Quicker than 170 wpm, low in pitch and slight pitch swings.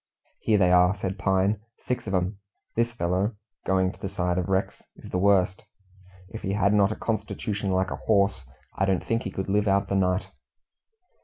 Yes: average, 200 wpm; very low, 95 Hz; narrow, 1.9 semitones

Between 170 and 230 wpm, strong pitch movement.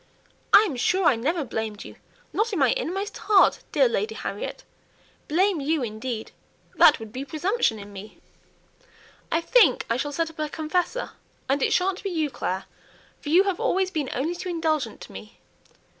Yes: average, 180 wpm; wide, 6.6 semitones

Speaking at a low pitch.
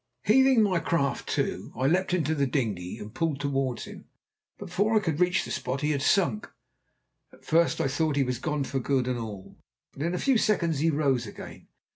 No: medium, 145 Hz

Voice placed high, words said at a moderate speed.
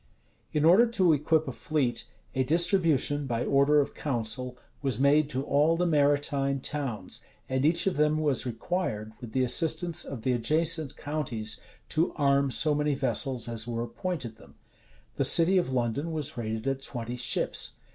No: medium, 140 Hz; average, 165 wpm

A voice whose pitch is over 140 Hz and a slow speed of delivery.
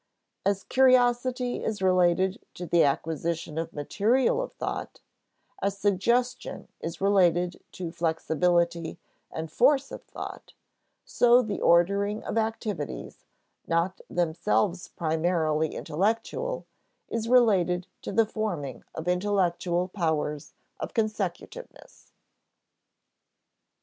Yes: medium, 185 Hz; slow, 100 wpm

